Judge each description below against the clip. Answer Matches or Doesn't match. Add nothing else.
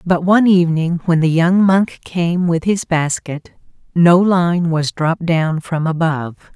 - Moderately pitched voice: Matches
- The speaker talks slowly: Doesn't match